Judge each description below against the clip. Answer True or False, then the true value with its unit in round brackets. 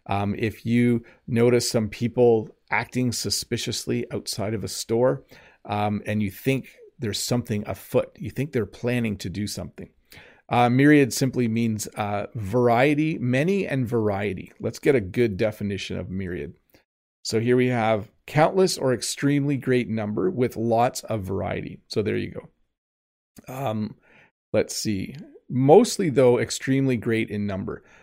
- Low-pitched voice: True (115 Hz)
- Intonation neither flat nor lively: True (3.5 semitones)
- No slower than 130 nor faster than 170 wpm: True (145 wpm)